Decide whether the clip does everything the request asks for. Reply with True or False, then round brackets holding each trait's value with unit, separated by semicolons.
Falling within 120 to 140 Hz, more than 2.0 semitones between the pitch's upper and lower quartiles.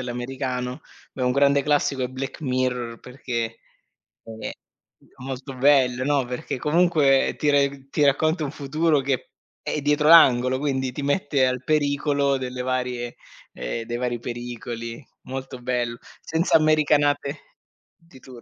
True (135 Hz; 2.5 semitones)